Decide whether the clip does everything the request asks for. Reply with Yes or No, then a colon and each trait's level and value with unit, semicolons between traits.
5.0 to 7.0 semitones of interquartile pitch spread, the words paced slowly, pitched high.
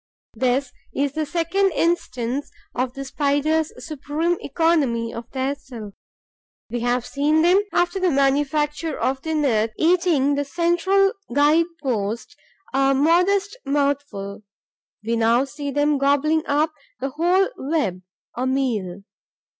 No: average, 3.8 semitones; slow, 130 wpm; very high, 285 Hz